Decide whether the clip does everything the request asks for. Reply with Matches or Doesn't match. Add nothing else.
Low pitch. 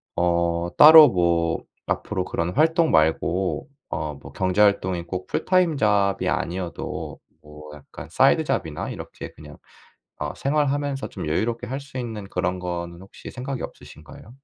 Matches